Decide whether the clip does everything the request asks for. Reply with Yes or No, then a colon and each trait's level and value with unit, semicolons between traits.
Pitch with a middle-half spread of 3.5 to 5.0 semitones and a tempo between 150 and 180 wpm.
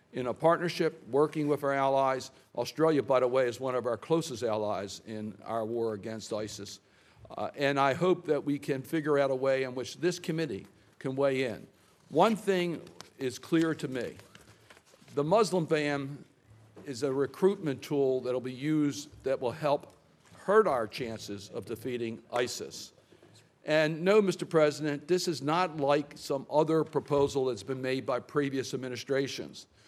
Yes: average, 3.8 semitones; average, 165 wpm